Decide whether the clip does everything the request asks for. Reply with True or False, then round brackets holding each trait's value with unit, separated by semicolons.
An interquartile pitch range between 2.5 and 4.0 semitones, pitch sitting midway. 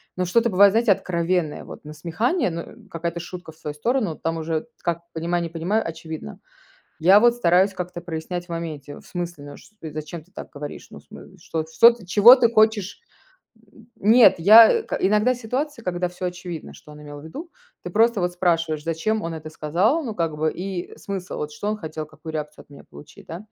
False (4.8 semitones; 175 Hz)